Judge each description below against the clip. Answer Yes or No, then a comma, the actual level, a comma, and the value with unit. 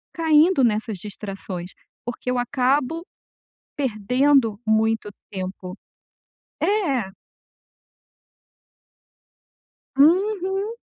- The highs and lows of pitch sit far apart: Yes, wide, 7.1 semitones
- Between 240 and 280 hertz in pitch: Yes, very high, 250 Hz